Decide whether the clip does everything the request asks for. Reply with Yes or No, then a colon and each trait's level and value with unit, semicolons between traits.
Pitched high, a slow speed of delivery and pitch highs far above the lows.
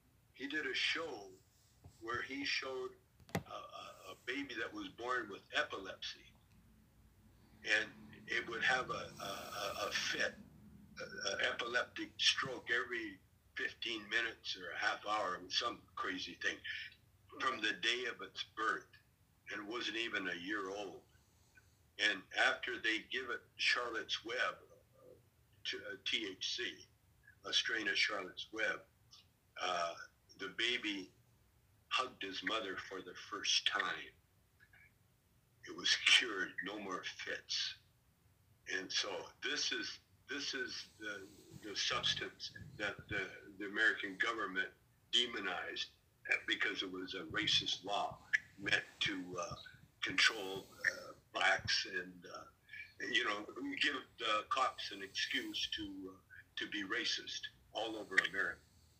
Yes: very high, 385 Hz; slow, 130 wpm; wide, 6.3 semitones